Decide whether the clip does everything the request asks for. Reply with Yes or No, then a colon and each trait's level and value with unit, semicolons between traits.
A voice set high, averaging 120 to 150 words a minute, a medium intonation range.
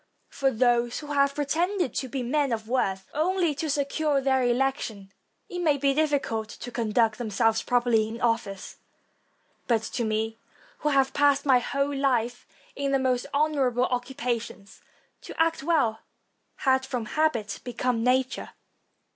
Yes: very high, 260 Hz; average, 145 wpm; average, 3.5 semitones